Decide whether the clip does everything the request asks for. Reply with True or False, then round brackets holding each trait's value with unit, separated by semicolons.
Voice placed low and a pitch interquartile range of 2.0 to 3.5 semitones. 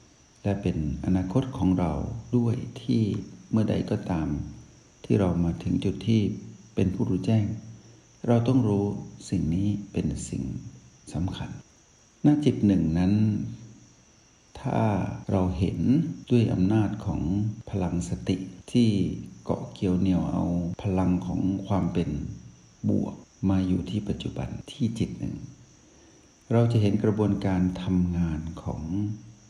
True (95 Hz; 3.1 semitones)